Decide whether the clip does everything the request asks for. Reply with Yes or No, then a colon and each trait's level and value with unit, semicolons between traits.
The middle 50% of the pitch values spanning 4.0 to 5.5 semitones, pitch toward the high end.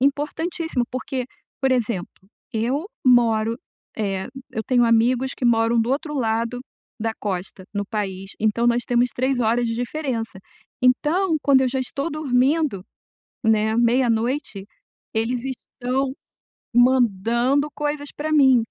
No: average, 3.1 semitones; high, 245 Hz